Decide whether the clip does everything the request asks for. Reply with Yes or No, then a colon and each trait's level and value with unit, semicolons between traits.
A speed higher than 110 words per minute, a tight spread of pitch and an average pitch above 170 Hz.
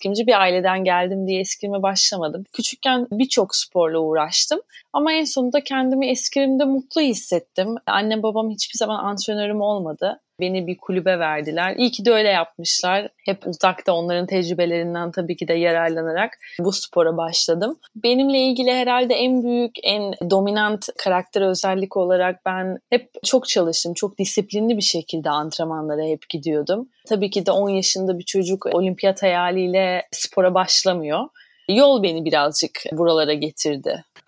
No: fast, 140 wpm; average, 4.2 semitones; high, 190 Hz